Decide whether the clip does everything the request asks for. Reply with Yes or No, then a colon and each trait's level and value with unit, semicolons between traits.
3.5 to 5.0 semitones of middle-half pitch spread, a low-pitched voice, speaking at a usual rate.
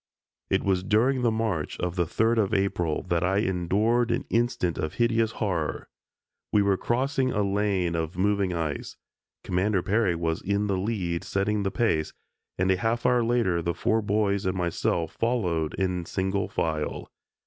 Yes: average, 4.3 semitones; low, 100 Hz; average, 170 wpm